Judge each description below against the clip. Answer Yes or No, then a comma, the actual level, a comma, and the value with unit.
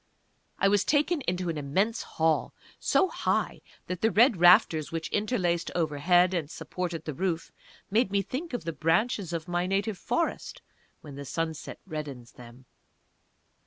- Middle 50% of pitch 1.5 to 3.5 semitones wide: No, average, 4.1 semitones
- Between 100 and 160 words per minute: Yes, average, 155 wpm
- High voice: No, medium, 175 Hz